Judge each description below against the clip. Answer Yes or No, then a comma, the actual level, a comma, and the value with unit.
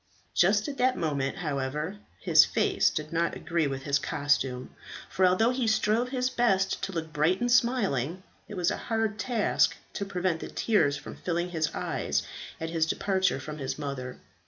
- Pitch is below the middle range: No, medium, 175 Hz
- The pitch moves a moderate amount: No, wide, 6.1 semitones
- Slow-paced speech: No, average, 180 wpm